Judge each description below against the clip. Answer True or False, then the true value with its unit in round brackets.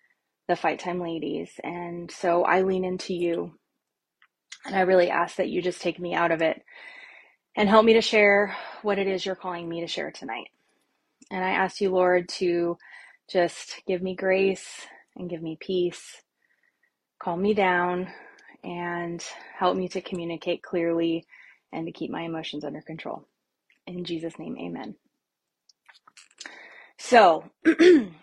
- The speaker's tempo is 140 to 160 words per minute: True (150 wpm)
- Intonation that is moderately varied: False (1.9 semitones)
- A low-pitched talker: False (180 Hz)